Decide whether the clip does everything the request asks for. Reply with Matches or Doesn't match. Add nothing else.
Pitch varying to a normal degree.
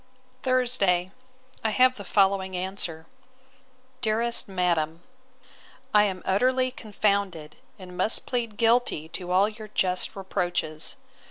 Matches